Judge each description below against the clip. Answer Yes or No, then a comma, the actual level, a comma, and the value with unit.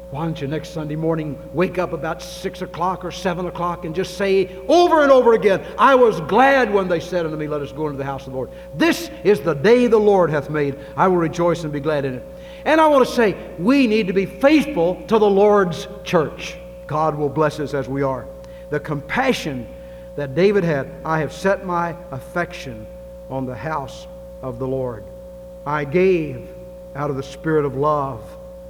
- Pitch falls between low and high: Yes, medium, 175 Hz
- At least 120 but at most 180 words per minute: No, fast, 205 wpm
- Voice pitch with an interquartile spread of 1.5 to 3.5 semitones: No, average, 4.4 semitones